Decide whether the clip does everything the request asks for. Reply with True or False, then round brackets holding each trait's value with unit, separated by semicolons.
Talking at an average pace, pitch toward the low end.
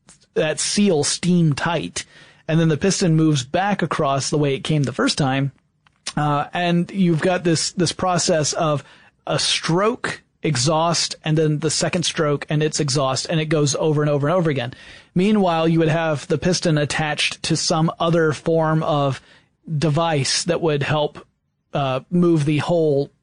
False (170 wpm; 160 Hz)